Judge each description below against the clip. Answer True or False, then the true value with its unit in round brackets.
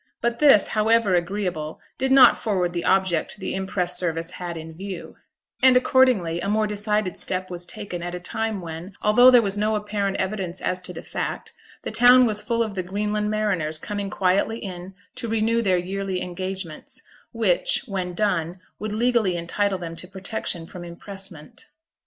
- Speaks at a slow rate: False (175 wpm)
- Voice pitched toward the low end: False (195 Hz)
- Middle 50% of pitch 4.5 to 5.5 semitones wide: False (3.3 semitones)